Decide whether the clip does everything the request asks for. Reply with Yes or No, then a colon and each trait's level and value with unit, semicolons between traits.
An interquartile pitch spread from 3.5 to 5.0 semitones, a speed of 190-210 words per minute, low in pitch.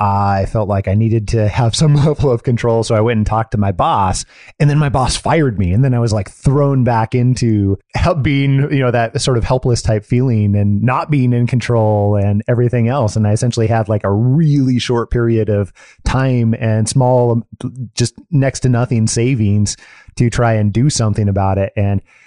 No: average, 3.0 semitones; fast, 205 wpm; low, 115 Hz